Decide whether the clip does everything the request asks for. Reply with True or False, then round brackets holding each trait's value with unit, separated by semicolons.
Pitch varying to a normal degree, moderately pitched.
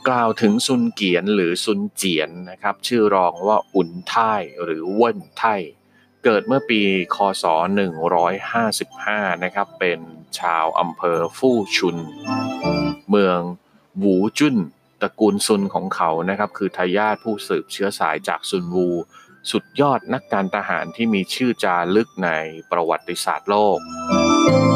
False (4.2 semitones; 100 Hz)